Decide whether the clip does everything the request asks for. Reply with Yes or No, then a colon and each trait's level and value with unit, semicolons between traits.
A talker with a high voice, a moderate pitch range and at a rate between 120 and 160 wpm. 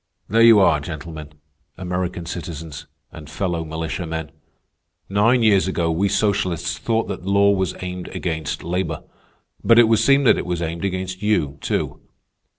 No: very low, 90 Hz; average, 3.7 semitones; average, 155 wpm